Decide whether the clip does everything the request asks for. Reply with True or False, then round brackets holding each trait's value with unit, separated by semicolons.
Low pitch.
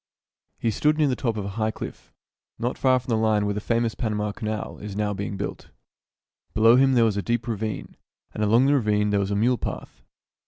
True (110 Hz)